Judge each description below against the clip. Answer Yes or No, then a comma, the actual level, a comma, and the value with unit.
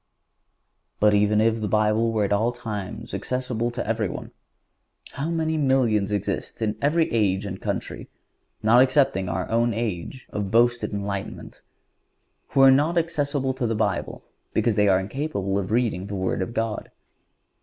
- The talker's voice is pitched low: Yes, low, 110 Hz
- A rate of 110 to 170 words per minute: Yes, average, 155 wpm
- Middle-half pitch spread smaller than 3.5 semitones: No, average, 4.2 semitones